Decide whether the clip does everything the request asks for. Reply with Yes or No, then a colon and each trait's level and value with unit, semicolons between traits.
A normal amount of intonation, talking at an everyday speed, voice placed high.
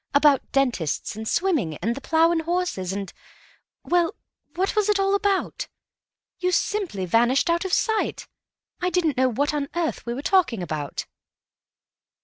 No: wide, 7.5 semitones; average, 150 wpm; very high, 305 Hz